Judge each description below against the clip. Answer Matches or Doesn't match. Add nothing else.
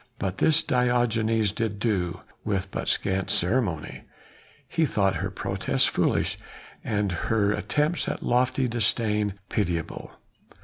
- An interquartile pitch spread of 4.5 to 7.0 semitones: Doesn't match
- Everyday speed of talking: Doesn't match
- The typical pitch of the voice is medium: Doesn't match